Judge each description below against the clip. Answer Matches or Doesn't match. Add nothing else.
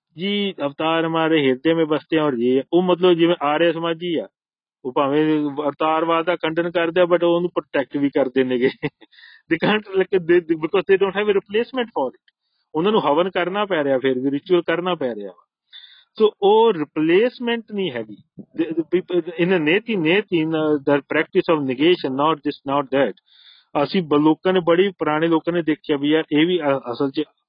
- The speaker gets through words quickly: Matches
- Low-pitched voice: Doesn't match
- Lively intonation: Doesn't match